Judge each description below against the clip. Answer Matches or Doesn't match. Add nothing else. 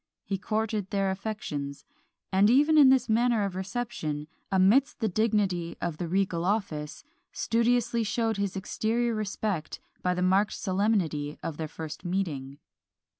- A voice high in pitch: Matches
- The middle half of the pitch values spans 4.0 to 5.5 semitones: Matches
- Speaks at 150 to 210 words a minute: Doesn't match